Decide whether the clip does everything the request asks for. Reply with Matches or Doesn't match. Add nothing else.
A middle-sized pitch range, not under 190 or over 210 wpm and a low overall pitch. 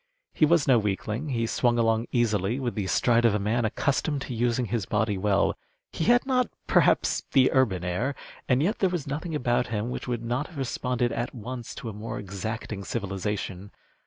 Matches